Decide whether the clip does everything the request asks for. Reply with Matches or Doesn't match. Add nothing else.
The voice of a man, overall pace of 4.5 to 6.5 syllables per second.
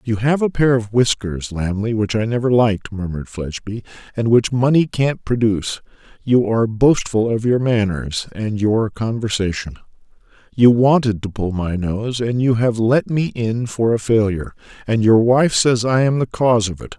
Matches